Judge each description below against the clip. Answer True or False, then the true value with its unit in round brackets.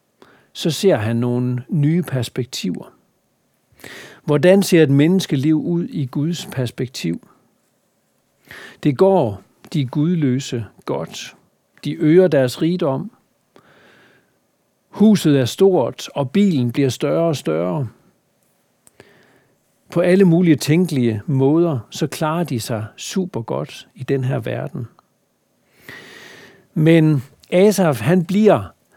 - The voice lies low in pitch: False (155 Hz)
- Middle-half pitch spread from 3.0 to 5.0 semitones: False (5.4 semitones)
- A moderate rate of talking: False (105 wpm)